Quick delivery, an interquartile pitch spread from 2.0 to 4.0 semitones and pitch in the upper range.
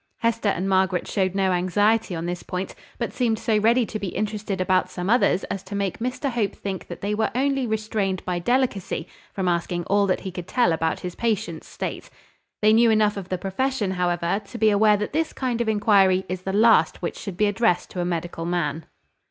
Yes: fast, 215 wpm; average, 3.3 semitones; high, 200 Hz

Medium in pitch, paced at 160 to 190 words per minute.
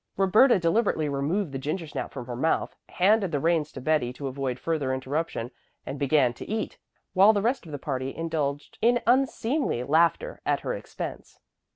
Yes: medium, 155 Hz; average, 175 wpm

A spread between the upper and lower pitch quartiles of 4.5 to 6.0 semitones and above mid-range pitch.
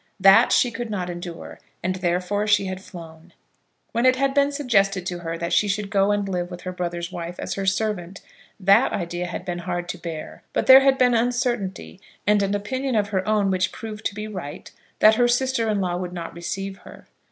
No: average, 3.7 semitones; high, 195 Hz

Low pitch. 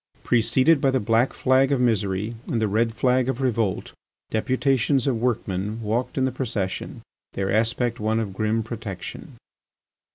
Yes: low, 115 Hz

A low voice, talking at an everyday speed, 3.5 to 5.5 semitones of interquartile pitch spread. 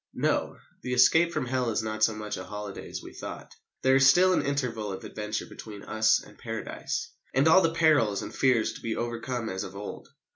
No: low, 115 Hz; fast, 215 wpm; average, 4.2 semitones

